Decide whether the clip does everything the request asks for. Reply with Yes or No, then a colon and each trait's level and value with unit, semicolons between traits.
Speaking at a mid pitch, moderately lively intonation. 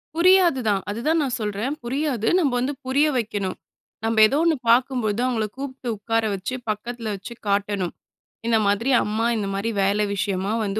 No: high, 225 Hz; average, 4.2 semitones